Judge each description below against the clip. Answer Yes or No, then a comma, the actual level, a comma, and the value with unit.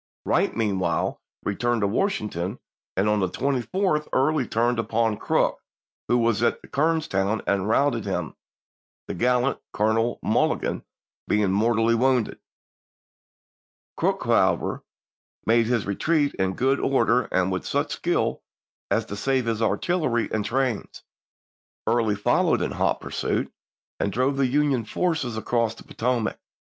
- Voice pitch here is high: No, low, 115 Hz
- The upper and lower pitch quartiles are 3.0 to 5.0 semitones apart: Yes, average, 4.0 semitones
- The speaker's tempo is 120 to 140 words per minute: Yes, slow, 135 wpm